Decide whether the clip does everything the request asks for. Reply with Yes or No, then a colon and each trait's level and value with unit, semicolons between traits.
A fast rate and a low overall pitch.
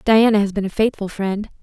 No: fast, 220 wpm; high, 205 Hz